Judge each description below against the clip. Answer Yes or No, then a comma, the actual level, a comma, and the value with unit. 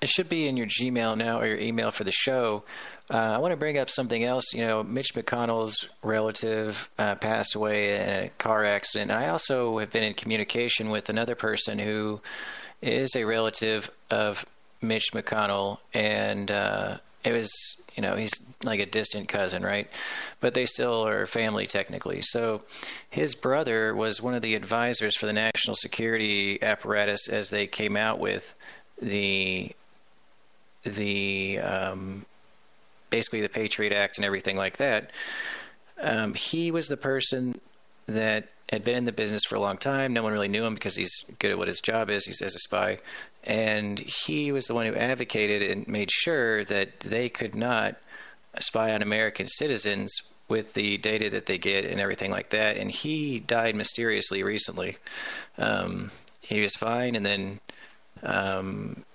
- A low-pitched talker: Yes, low, 110 Hz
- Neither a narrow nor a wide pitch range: No, narrow, 2.1 semitones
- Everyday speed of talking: Yes, average, 170 wpm